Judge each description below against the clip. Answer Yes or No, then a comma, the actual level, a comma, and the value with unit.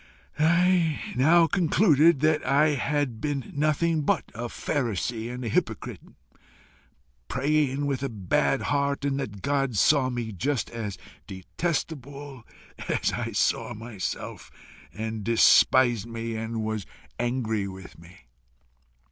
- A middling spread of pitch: Yes, average, 4.7 semitones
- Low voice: Yes, low, 130 Hz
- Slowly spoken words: Yes, slow, 120 wpm